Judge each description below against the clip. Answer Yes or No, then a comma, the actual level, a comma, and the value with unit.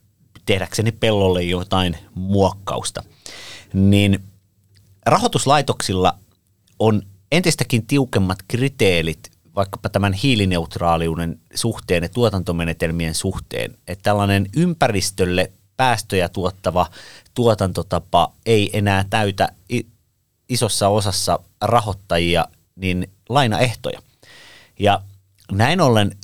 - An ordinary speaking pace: No, slow, 80 wpm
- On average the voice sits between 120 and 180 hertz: No, low, 100 Hz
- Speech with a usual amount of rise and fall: Yes, average, 3.4 semitones